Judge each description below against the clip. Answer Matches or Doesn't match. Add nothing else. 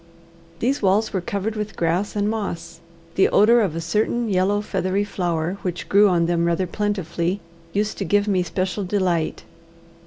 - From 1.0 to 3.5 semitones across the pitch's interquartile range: Matches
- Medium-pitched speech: Doesn't match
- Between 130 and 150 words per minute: Doesn't match